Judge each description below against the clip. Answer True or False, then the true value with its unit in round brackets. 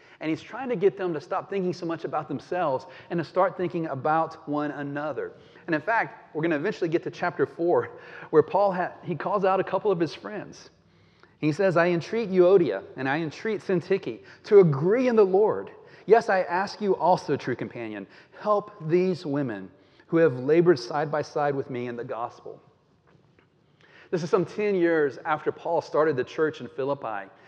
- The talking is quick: False (195 wpm)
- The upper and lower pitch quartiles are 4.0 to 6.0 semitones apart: True (4.7 semitones)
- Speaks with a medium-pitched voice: True (170 Hz)